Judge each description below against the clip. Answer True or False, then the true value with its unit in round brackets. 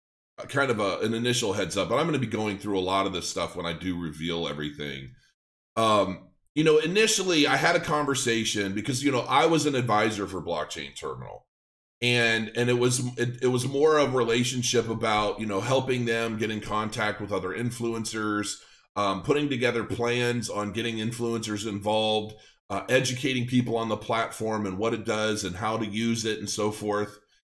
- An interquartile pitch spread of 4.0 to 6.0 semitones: False (2.8 semitones)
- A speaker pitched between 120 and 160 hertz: False (110 Hz)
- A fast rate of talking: False (195 wpm)